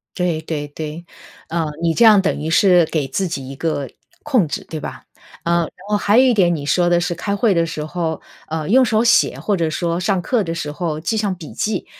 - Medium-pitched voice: Yes, medium, 170 Hz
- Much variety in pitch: No, average, 4.2 semitones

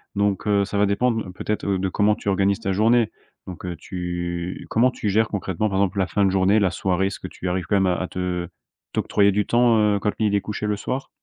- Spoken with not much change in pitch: Yes, narrow, 2.2 semitones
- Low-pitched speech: Yes, low, 100 Hz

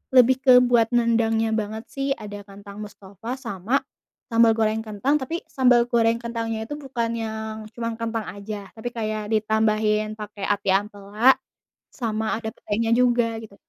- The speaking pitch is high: Yes, high, 220 Hz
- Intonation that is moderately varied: No, narrow, 1.7 semitones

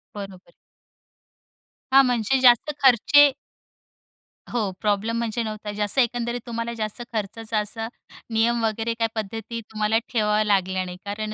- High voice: Yes, high, 225 Hz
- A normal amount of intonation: No, narrow, 2.0 semitones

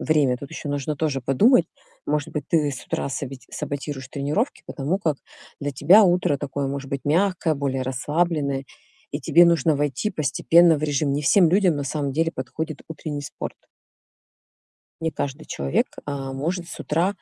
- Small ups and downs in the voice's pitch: No, average, 3.0 semitones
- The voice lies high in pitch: No, medium, 145 Hz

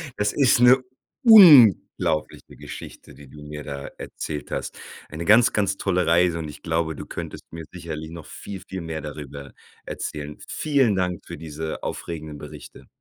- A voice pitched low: Yes, very low, 80 Hz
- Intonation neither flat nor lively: Yes, average, 4.6 semitones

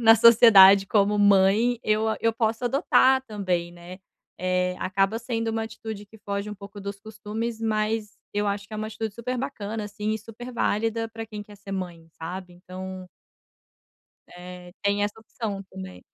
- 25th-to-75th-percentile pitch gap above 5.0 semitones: No, narrow, 2.6 semitones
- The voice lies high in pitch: Yes, high, 210 Hz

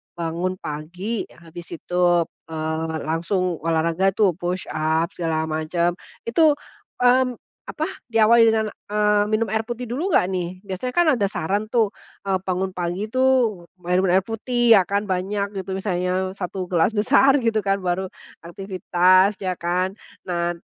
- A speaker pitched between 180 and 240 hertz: Yes, high, 190 Hz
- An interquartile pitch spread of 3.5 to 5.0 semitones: Yes, average, 3.8 semitones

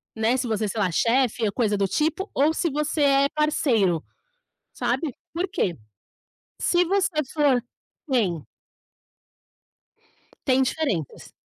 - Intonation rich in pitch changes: Yes, wide, 6.2 semitones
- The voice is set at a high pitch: Yes, very high, 260 Hz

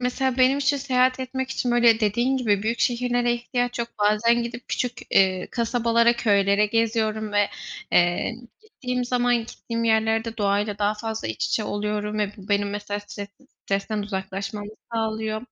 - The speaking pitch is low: No, high, 225 Hz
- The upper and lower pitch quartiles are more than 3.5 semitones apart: No, average, 2.8 semitones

